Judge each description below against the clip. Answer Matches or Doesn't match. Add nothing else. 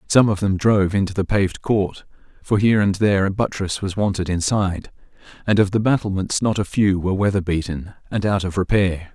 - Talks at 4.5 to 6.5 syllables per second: Matches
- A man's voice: Matches